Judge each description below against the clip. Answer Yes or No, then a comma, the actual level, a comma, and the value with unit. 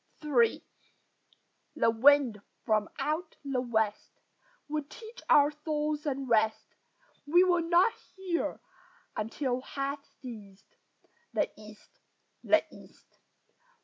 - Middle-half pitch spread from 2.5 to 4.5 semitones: No, average, 5.3 semitones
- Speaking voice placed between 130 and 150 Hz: No, very high, 275 Hz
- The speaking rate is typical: No, slow, 100 wpm